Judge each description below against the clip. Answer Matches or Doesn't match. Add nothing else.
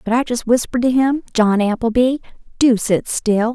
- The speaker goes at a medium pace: Matches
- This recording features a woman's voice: Matches